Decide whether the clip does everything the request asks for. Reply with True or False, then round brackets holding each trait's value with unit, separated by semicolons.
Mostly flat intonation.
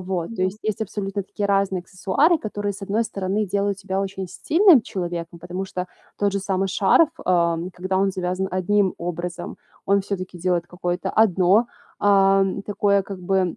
True (1.8 semitones)